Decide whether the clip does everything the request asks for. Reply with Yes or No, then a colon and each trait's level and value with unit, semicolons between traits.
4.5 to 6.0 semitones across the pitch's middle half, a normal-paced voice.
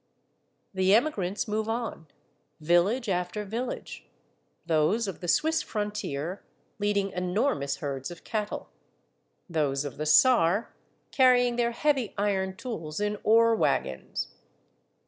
No: average, 5.1 semitones; slow, 115 wpm